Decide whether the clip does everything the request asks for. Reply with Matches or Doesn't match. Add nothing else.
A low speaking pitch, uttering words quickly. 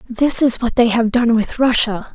Doesn't match